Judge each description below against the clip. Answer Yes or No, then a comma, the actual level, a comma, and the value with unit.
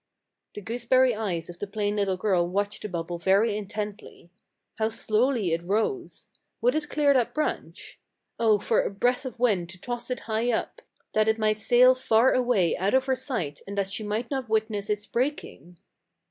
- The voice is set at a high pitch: Yes, high, 215 Hz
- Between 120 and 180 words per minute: No, average, 190 wpm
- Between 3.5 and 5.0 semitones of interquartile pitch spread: Yes, average, 3.8 semitones